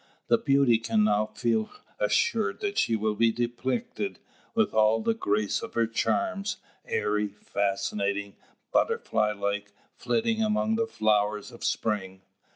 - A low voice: Yes, low, 110 Hz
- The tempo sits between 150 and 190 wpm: No, slow, 135 wpm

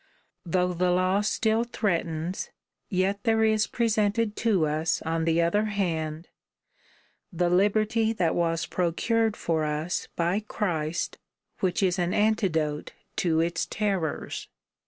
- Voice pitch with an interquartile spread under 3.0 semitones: No, average, 4.1 semitones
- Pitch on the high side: No, medium, 180 Hz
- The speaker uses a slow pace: Yes, slow, 125 wpm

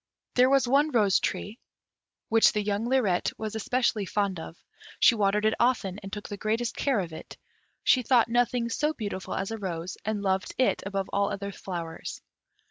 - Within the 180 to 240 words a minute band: Yes, average, 185 wpm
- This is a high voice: Yes, high, 210 Hz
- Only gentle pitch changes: No, average, 3.6 semitones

